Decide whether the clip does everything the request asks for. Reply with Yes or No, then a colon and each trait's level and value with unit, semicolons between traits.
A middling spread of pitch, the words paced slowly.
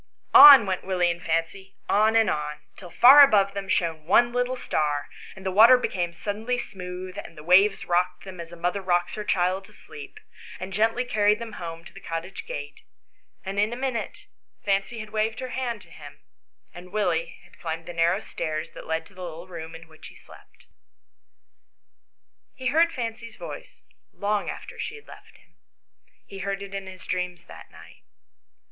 No: average, 4.2 semitones; average, 190 wpm